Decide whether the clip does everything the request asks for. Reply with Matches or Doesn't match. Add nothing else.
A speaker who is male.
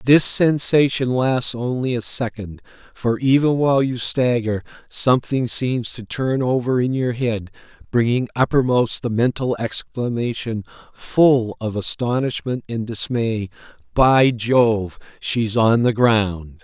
Matches